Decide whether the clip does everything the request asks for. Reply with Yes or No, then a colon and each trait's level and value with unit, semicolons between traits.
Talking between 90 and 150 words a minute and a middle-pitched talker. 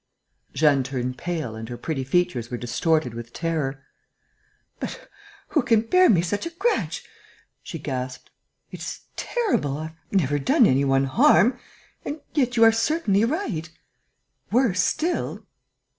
Yes: average, 145 wpm; medium, 165 Hz